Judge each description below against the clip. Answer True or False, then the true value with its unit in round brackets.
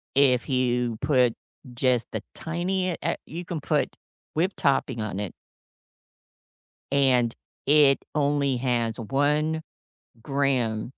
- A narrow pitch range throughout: False (3.6 semitones)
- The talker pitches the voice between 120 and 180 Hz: True (135 Hz)